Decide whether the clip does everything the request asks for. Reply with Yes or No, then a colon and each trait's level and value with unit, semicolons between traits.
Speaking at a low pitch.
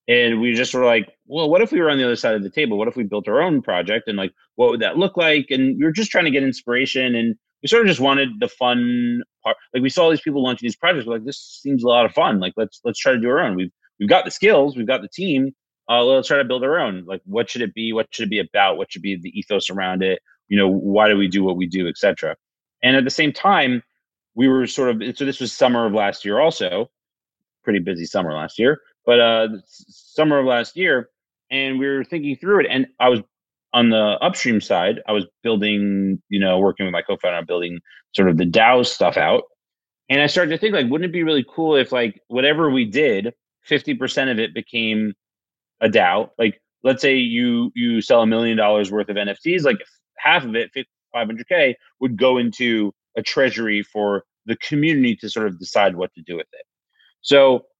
Yes: low, 120 Hz